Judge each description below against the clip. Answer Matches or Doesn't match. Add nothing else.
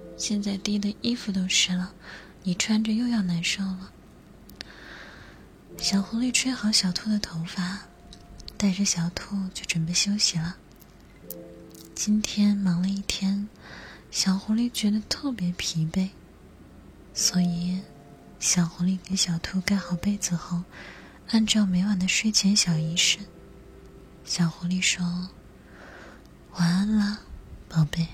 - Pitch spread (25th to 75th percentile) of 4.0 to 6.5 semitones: Doesn't match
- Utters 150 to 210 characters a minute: Matches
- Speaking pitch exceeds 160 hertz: Matches